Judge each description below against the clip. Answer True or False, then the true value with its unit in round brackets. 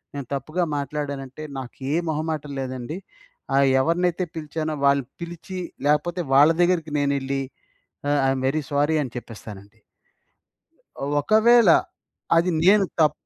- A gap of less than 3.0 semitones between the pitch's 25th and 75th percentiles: False (3.6 semitones)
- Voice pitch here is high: False (150 Hz)